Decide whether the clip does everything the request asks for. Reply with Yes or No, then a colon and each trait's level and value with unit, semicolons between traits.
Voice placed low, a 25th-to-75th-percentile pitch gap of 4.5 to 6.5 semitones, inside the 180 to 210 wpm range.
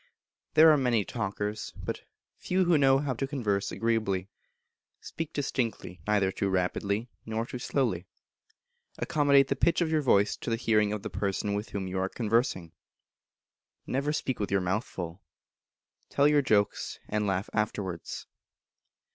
No: low, 110 Hz; wide, 5.5 semitones; average, 155 wpm